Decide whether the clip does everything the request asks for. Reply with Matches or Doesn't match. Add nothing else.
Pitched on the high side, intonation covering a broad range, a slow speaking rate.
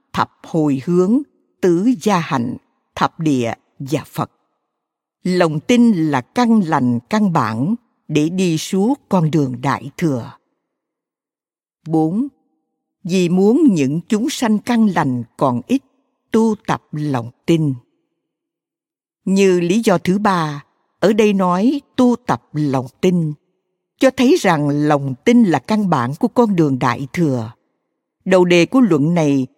Doesn't match